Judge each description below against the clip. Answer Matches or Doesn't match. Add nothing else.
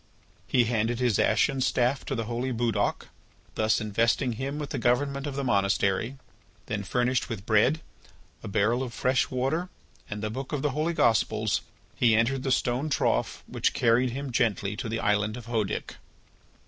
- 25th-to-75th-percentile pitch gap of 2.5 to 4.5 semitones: Matches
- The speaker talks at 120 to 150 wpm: Doesn't match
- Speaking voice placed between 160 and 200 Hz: Doesn't match